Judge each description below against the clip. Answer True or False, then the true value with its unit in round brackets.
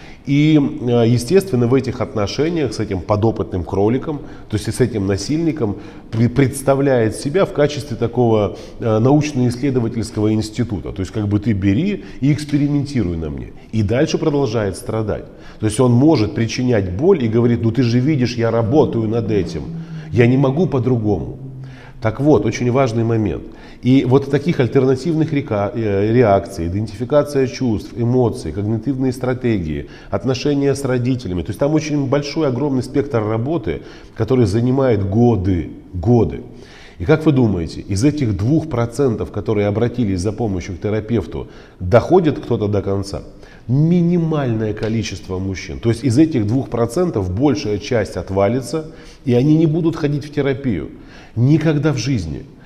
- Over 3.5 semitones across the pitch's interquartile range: True (4.8 semitones)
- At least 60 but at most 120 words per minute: False (140 wpm)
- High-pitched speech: False (120 Hz)